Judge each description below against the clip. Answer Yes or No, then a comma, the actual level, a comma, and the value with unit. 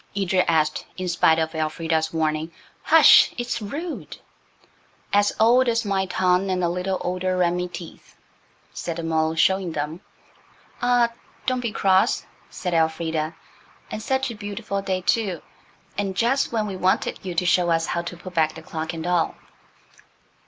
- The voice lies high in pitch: No, medium, 180 Hz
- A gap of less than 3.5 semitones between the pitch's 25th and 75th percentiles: No, average, 3.8 semitones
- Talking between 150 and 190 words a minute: Yes, average, 160 wpm